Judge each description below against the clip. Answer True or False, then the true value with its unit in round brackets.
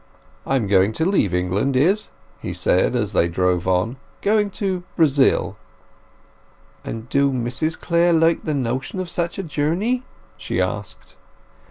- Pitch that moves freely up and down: True (8.2 semitones)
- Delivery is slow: False (150 wpm)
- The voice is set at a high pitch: False (140 Hz)